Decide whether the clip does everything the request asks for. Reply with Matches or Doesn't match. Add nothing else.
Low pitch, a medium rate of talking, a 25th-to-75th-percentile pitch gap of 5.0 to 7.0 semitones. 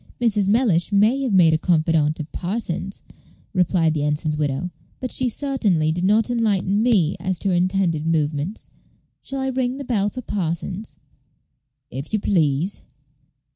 Doesn't match